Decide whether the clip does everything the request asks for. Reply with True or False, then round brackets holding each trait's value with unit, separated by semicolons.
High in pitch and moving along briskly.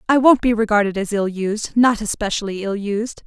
True (215 Hz; 220 wpm)